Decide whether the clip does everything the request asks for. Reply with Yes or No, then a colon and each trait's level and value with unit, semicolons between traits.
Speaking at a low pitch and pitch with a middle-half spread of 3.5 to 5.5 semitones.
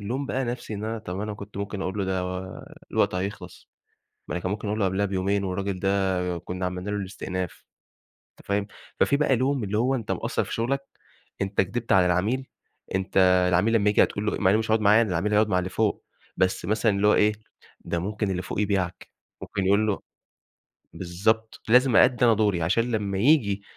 No: low, 100 Hz; average, 2.8 semitones